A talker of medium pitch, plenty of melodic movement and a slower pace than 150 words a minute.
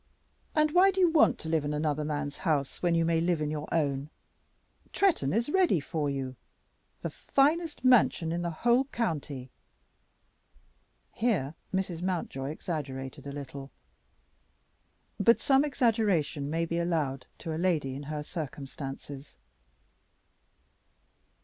Yes: medium, 160 Hz; wide, 7.3 semitones; slow, 135 wpm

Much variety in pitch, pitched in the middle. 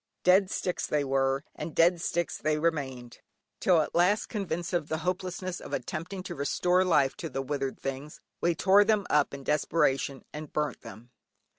No: average, 4.5 semitones; medium, 160 Hz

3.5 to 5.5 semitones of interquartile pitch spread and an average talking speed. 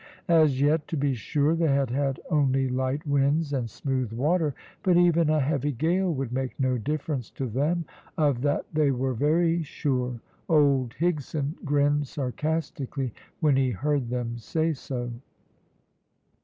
No: average, 3.0 semitones; average, 150 wpm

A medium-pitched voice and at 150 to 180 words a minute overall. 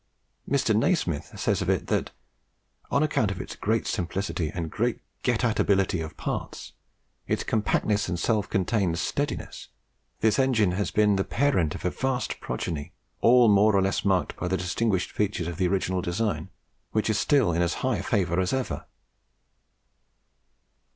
No: low, 100 Hz; average, 160 wpm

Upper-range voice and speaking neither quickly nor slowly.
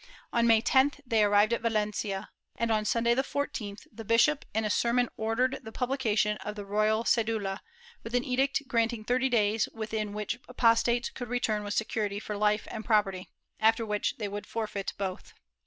Yes: high, 220 Hz; average, 180 wpm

